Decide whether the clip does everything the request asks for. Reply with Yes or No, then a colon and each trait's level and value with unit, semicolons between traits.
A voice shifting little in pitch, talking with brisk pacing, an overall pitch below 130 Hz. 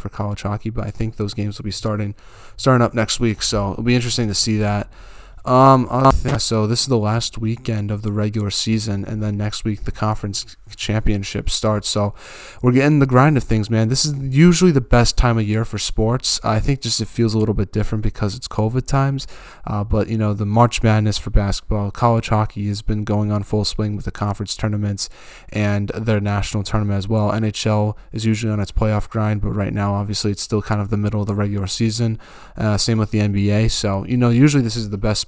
Yes: narrow, 1.8 semitones; fast, 225 wpm; low, 110 Hz